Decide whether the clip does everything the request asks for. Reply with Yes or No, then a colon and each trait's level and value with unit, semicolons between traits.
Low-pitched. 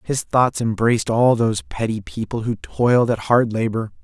Yes: low, 115 Hz